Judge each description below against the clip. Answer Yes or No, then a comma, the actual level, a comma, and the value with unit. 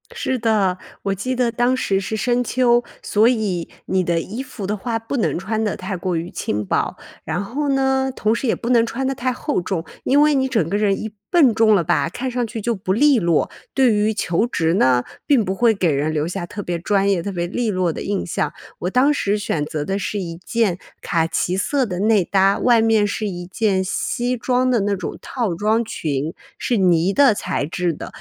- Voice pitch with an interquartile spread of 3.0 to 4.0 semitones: No, average, 5.0 semitones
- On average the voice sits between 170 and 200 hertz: No, high, 210 Hz